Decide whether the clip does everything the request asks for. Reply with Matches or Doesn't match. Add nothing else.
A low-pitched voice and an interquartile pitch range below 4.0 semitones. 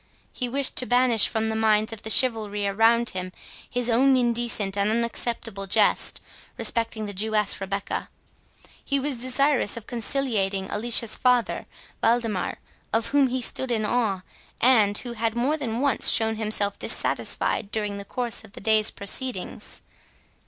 Doesn't match